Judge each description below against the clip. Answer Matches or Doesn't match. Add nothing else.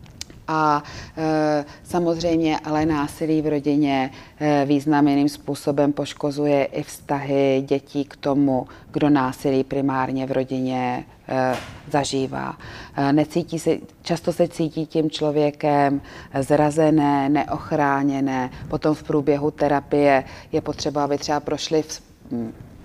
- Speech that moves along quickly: Doesn't match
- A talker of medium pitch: Matches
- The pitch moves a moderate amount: Doesn't match